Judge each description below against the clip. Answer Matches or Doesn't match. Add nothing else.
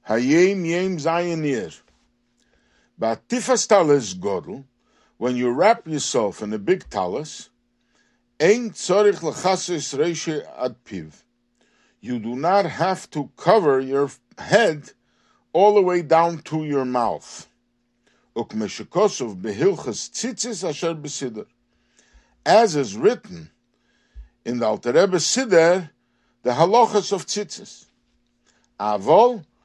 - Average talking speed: Doesn't match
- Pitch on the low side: Doesn't match